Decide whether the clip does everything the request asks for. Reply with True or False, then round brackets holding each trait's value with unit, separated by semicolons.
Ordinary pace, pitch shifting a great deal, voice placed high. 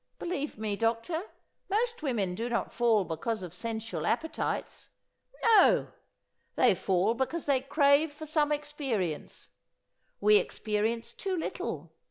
False (125 wpm; 6.2 semitones; 240 Hz)